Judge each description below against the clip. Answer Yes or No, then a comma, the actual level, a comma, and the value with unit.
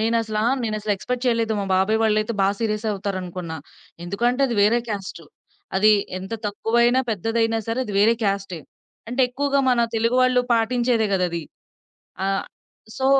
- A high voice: Yes, high, 220 Hz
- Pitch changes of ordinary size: Yes, average, 3.1 semitones